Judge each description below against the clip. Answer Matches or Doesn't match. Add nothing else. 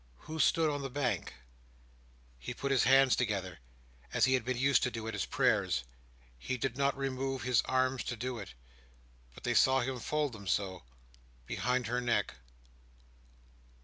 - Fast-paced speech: Doesn't match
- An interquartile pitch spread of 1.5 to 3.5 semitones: Matches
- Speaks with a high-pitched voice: Doesn't match